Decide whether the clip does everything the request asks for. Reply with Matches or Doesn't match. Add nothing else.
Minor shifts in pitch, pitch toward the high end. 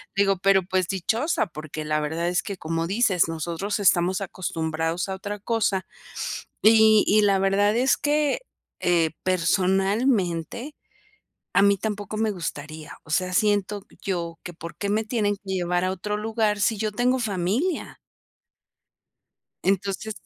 Doesn't match